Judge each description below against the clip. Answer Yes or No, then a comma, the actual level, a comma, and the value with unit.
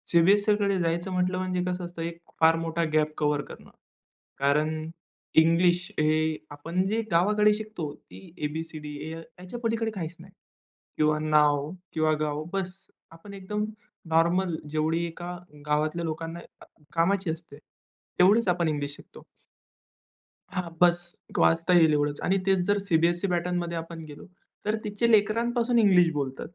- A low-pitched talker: No, medium, 170 Hz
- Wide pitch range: No, average, 3.2 semitones